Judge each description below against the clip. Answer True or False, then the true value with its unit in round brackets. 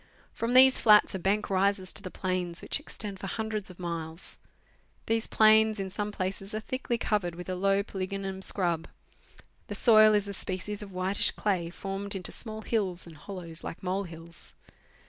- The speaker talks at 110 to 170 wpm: False (180 wpm)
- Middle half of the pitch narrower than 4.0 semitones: True (2.5 semitones)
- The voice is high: True (195 Hz)